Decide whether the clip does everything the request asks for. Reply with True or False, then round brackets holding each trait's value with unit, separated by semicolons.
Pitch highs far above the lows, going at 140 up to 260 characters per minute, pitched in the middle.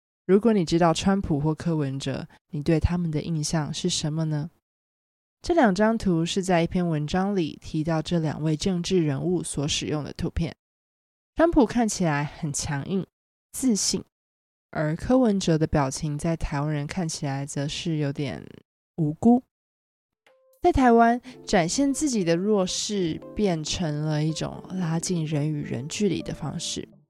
False (4.4 semitones; 230 characters per minute; 165 Hz)